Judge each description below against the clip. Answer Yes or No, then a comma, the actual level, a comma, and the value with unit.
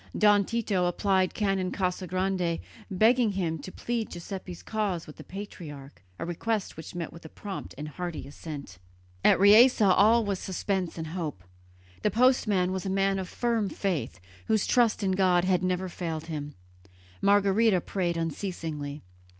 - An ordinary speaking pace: Yes, average, 160 wpm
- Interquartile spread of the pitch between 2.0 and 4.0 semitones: Yes, average, 3.3 semitones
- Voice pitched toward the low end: No, medium, 185 Hz